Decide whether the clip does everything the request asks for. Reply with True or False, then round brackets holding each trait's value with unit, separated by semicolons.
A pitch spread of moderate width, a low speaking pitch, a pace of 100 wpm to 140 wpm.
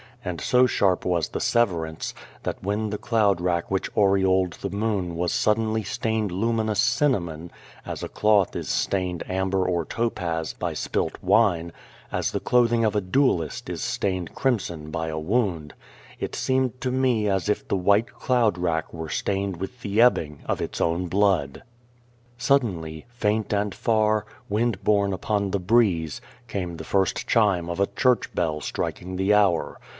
False (4.1 semitones; 100 Hz; 165 wpm)